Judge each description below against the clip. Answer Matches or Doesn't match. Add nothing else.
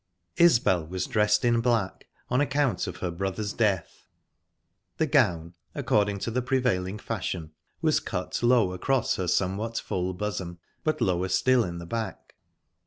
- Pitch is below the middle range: Matches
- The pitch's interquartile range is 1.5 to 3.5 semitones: Doesn't match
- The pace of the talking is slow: Doesn't match